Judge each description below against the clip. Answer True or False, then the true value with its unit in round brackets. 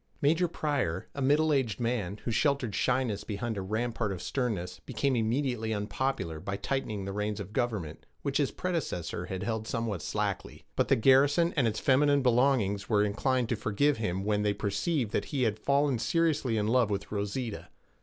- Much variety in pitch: False (4.8 semitones)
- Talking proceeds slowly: False (180 wpm)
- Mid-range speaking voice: False (115 Hz)